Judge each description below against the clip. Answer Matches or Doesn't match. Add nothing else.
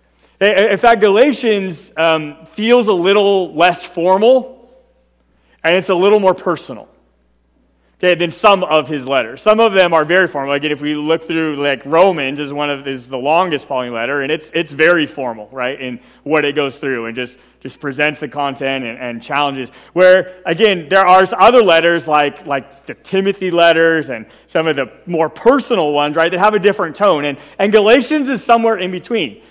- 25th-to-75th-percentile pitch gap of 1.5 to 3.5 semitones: Doesn't match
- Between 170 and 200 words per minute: Matches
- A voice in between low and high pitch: Matches